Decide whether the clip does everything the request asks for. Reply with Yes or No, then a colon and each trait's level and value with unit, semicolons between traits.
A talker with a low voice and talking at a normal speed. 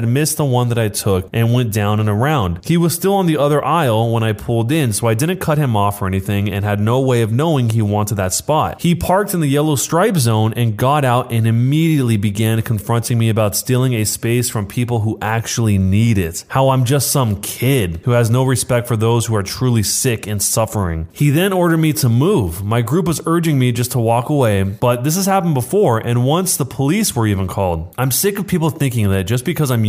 No: low, 120 Hz; fast, 235 wpm